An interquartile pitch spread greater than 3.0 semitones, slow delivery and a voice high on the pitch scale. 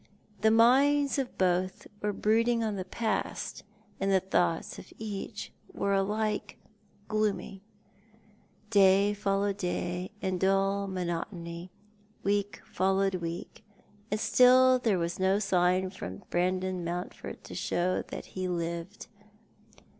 No: narrow, 2.5 semitones; slow, 125 wpm; high, 195 Hz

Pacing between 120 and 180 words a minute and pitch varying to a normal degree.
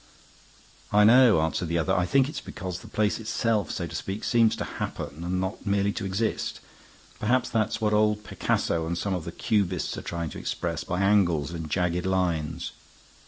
No: average, 190 wpm; average, 3.8 semitones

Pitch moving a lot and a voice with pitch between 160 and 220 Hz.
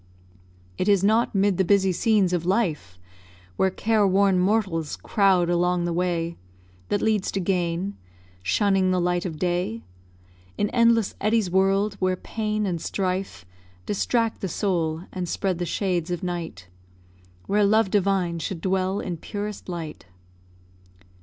No: narrow, 2.6 semitones; high, 190 Hz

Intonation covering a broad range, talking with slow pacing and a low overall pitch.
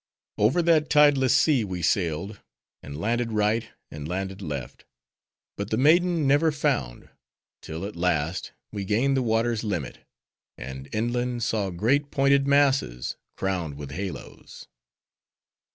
Yes: wide, 7.7 semitones; slow, 130 wpm; low, 110 Hz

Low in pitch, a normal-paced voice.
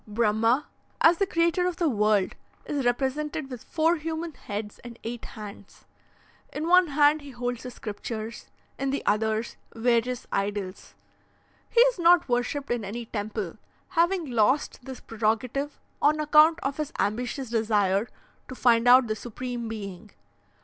No: high, 245 Hz; average, 150 wpm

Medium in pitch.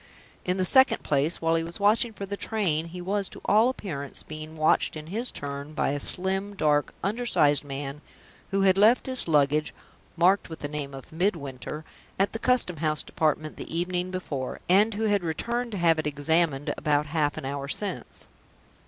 Yes: medium, 165 Hz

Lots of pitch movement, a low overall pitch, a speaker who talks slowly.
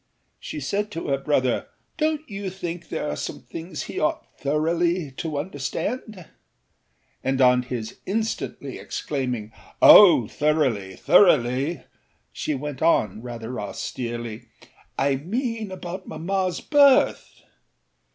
No: wide, 6.8 semitones; medium, 150 Hz; slow, 110 wpm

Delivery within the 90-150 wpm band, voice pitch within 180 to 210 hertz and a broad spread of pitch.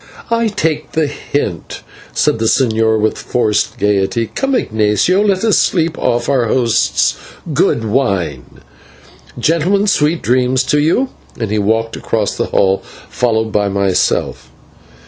No: slow, 135 wpm; low, 120 Hz; wide, 6.9 semitones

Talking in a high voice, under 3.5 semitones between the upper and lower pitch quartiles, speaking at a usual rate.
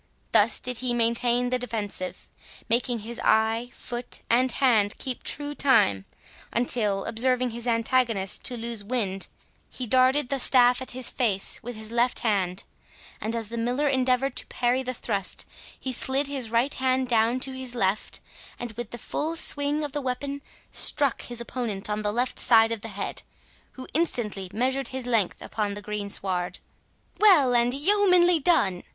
Yes: high, 245 Hz; average, 2.9 semitones; average, 170 wpm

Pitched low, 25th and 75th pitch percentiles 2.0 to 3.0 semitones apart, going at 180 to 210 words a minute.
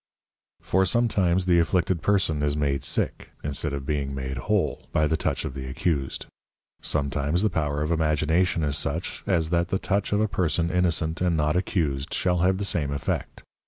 No: very low, 80 Hz; average, 3.8 semitones; average, 190 wpm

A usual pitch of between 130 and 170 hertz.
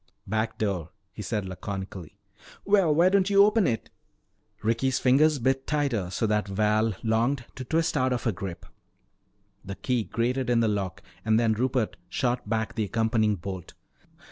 No: low, 115 Hz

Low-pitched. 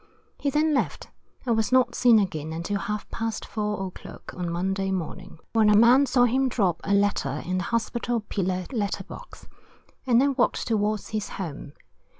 No: high, 210 Hz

